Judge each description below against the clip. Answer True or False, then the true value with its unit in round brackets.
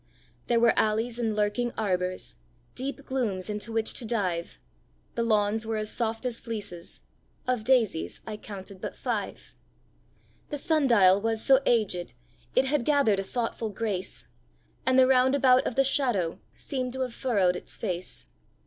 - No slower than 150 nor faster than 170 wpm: True (160 wpm)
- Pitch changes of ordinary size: True (3.9 semitones)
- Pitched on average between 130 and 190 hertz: False (225 Hz)